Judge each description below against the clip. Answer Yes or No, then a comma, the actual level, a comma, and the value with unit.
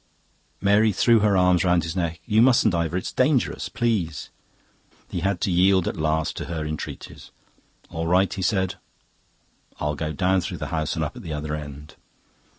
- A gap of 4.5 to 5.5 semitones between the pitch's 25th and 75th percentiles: No, average, 3.8 semitones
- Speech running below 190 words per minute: Yes, average, 180 wpm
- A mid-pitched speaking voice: No, very low, 90 Hz